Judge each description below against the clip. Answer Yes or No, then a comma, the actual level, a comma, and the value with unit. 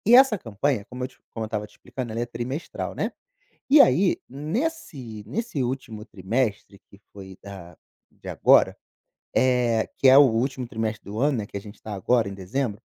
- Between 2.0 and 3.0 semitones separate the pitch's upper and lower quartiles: No, average, 4.3 semitones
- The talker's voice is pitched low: Yes, low, 120 Hz